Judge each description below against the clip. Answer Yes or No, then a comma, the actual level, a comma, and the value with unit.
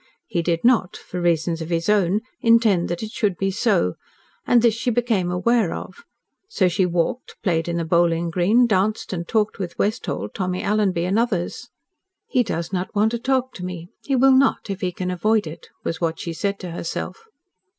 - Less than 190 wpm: No, average, 200 wpm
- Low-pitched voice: No, medium, 185 Hz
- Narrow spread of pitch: No, average, 4.5 semitones